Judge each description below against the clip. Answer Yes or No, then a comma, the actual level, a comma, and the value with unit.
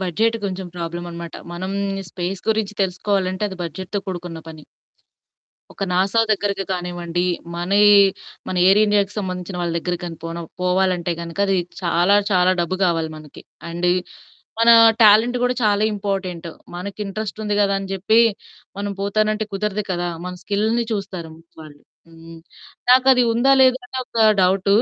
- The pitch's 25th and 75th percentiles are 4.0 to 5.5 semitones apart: No, average, 2.9 semitones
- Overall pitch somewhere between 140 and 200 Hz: Yes, high, 190 Hz